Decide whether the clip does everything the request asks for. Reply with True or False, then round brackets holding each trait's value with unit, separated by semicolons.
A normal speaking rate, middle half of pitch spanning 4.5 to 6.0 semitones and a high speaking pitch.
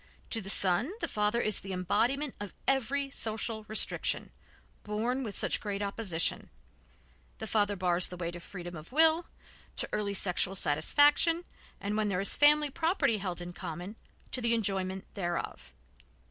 True (160 wpm; 5.2 semitones; 210 Hz)